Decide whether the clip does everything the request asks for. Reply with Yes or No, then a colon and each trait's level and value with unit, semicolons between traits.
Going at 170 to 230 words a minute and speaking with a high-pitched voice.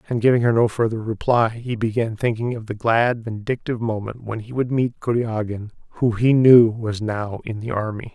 No: average, 200 wpm; low, 115 Hz